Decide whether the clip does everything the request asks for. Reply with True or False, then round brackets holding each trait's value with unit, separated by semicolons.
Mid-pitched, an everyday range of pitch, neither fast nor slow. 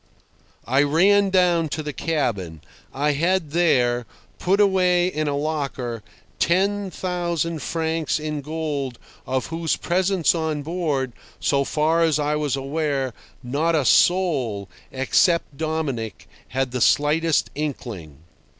False (155 Hz; 3.8 semitones; 125 wpm)